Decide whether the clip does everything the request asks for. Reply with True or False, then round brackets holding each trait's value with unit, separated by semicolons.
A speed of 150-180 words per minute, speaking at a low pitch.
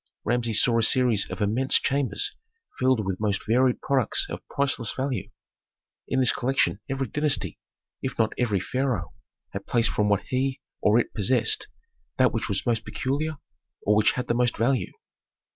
True (165 wpm; 120 Hz)